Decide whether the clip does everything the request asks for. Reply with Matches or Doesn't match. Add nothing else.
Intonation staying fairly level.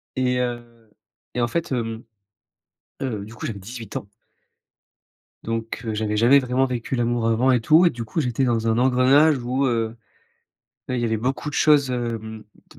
Matches